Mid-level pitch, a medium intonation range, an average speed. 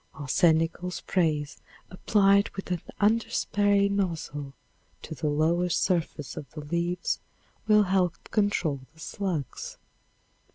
No: medium, 175 Hz; average, 4.2 semitones; slow, 110 wpm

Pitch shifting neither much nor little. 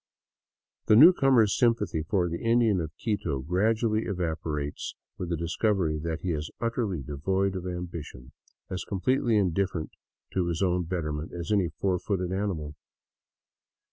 Yes: average, 4.3 semitones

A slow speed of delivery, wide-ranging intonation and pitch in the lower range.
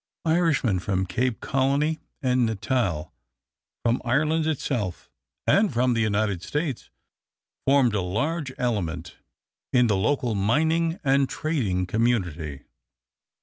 Yes: slow, 110 wpm; wide, 6.4 semitones; low, 120 Hz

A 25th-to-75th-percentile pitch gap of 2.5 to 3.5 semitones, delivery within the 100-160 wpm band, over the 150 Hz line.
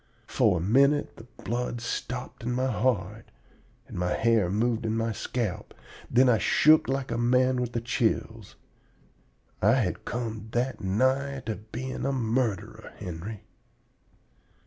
No: average, 2.9 semitones; average, 140 wpm; low, 120 Hz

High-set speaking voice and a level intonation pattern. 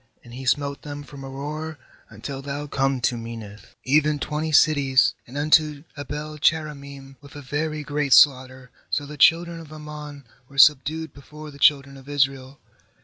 No: medium, 145 Hz; narrow, 1.9 semitones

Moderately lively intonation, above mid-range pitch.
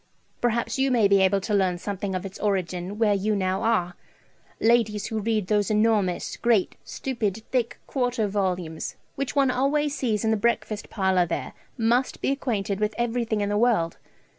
Yes: average, 3.3 semitones; high, 215 Hz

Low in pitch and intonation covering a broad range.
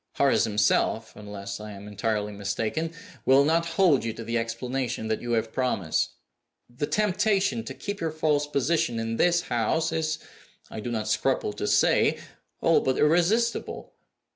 Yes: low, 125 Hz; wide, 6.7 semitones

